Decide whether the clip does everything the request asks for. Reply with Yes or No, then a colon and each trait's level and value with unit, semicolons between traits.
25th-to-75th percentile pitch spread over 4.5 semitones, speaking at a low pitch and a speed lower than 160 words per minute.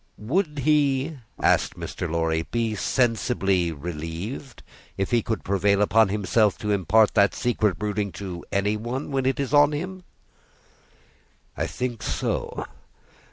Yes: average, 5.3 semitones; low, 110 Hz; slow, 135 wpm